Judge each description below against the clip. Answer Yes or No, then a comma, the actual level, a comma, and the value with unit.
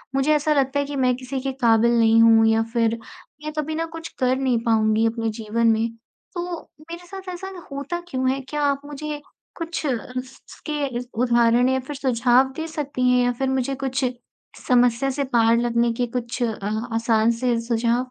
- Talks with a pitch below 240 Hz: No, very high, 255 Hz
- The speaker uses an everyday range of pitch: Yes, average, 3.5 semitones